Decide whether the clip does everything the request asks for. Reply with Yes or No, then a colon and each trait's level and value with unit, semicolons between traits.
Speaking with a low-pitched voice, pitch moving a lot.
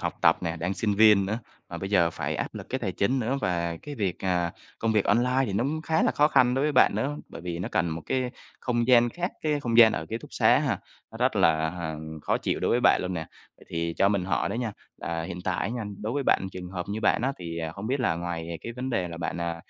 Yes: low, 100 Hz; wide, 6.2 semitones